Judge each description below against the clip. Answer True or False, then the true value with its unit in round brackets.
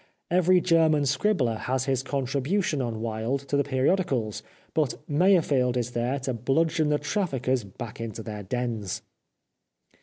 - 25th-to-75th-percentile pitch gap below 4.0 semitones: False (4.5 semitones)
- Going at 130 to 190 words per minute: True (140 wpm)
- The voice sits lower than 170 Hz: True (135 Hz)